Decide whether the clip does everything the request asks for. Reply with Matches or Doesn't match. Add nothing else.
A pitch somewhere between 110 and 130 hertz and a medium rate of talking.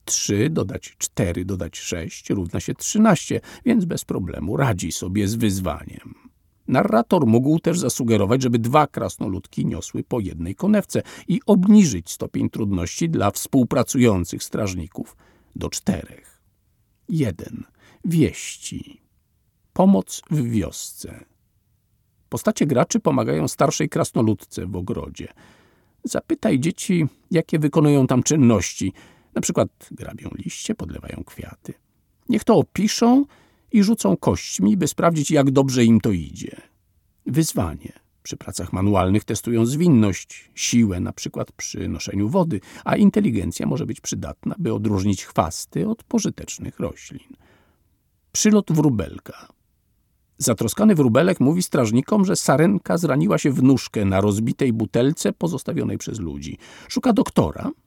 Matches